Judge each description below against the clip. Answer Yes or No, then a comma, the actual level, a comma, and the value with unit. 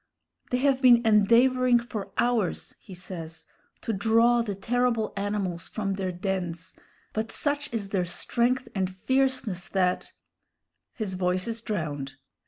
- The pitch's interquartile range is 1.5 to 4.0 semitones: No, average, 4.5 semitones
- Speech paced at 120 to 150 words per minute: Yes, average, 140 wpm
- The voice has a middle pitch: No, high, 210 Hz